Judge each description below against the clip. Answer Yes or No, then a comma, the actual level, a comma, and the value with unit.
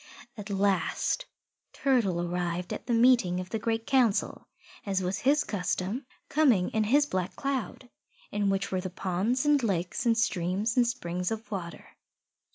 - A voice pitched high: Yes, high, 205 Hz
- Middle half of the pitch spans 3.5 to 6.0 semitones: Yes, average, 5.1 semitones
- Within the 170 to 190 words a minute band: No, average, 160 wpm